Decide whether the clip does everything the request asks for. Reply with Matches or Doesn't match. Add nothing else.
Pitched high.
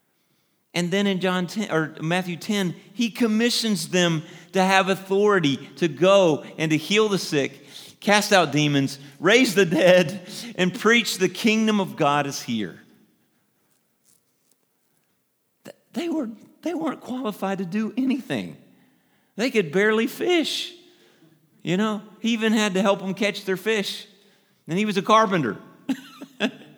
Matches